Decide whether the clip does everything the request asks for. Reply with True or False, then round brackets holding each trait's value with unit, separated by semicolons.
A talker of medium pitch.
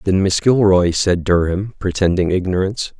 False (95 Hz)